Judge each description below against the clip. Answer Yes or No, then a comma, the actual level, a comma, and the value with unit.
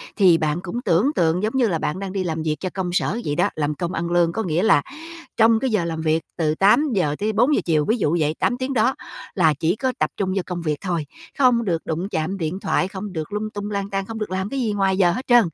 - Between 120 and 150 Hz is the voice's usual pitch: No, high, 190 Hz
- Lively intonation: No, average, 4.7 semitones